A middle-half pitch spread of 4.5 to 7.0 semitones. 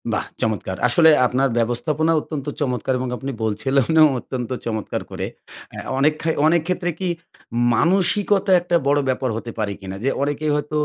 Yes: average, 4.8 semitones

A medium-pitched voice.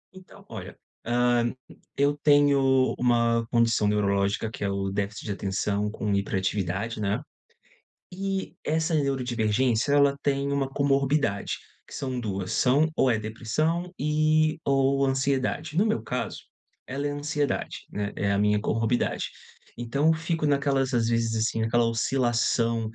No: low, 125 Hz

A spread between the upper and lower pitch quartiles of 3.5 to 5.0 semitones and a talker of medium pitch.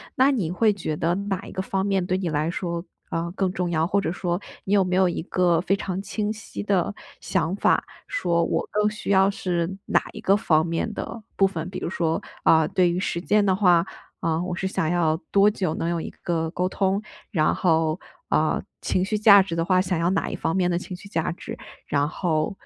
No: average, 2.7 semitones; medium, 180 Hz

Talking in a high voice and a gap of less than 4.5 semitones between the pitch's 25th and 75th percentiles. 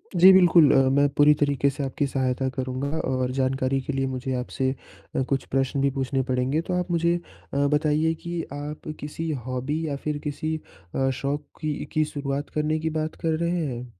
No: medium, 145 Hz; average, 2.8 semitones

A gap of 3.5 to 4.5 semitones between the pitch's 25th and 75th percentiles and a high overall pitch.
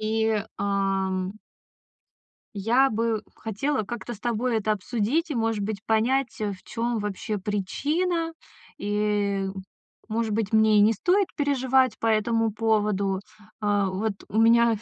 No: narrow, 2.5 semitones; high, 220 Hz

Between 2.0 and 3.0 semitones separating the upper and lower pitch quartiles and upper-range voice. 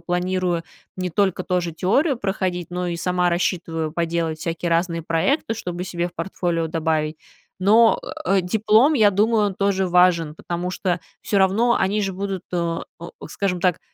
No: narrow, 2.6 semitones; medium, 180 Hz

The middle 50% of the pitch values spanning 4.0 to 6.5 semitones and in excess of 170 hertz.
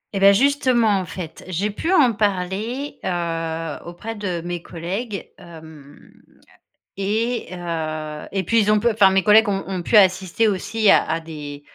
Yes: average, 4.4 semitones; high, 190 Hz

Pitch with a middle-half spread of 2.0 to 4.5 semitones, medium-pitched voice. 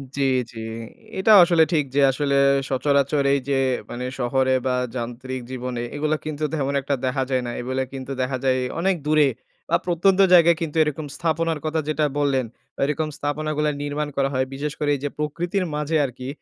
Yes: average, 2.9 semitones; medium, 145 Hz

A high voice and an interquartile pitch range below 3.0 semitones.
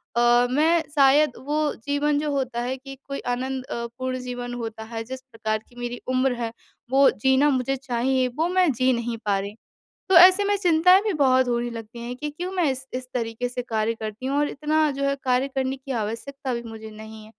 No: very high, 255 Hz; average, 3.3 semitones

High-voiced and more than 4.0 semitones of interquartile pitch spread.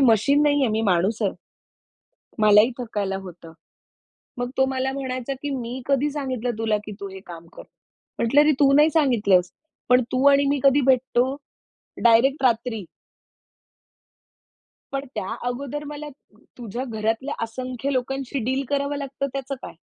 No: very high, 255 Hz; average, 3.7 semitones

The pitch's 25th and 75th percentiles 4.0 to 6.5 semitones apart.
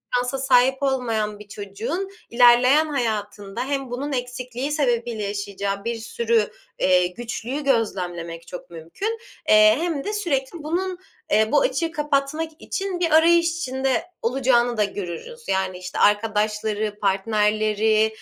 Yes: average, 5.1 semitones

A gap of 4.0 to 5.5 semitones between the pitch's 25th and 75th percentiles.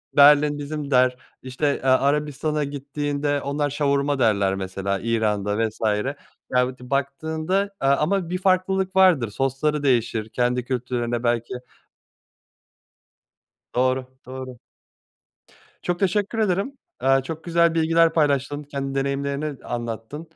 No: average, 3.5 semitones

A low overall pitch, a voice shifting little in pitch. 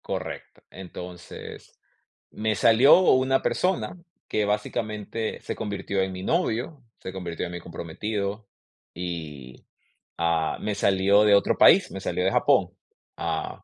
No: low, 100 Hz; average, 3.6 semitones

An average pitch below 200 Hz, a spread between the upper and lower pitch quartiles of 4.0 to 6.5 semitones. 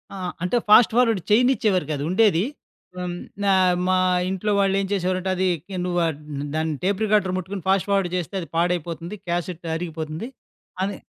No: medium, 185 Hz; narrow, 2.4 semitones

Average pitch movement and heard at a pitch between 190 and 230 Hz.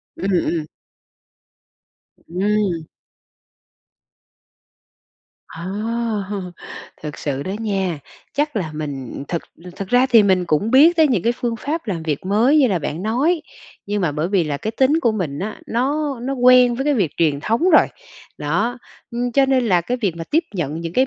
No: wide, 6.9 semitones; high, 210 Hz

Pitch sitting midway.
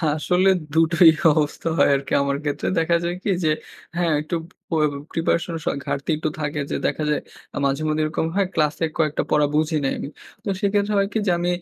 Yes: medium, 160 Hz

